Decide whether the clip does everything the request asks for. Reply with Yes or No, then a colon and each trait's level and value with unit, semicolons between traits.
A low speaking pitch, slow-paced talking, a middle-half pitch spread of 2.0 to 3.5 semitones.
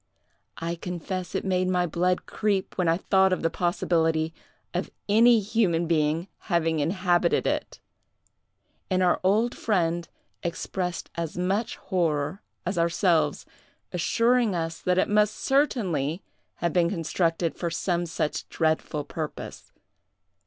No: medium, 175 Hz; slow, 130 wpm; narrow, 2.5 semitones